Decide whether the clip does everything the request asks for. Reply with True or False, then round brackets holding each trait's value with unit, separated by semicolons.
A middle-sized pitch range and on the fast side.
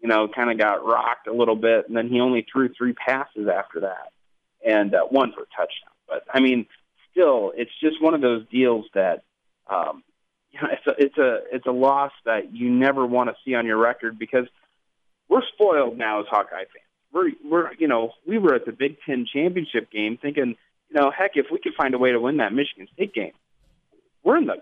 True (3.3 semitones; 225 wpm)